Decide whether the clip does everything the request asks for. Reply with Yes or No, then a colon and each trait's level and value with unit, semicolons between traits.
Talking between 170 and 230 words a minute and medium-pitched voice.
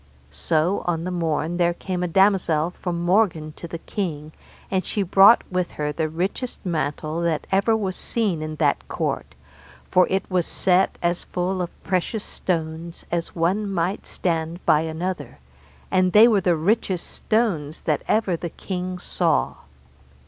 No: average, 160 wpm; medium, 175 Hz